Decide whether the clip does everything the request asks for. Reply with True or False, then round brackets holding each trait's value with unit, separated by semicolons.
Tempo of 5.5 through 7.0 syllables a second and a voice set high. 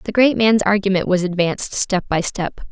False (5.1 syllables/s; 195 Hz)